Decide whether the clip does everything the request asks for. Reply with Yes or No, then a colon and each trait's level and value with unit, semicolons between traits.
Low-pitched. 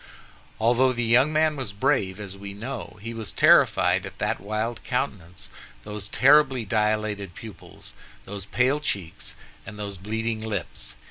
Yes: low, 110 Hz